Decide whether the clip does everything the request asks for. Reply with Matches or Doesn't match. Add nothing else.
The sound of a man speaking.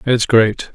Matches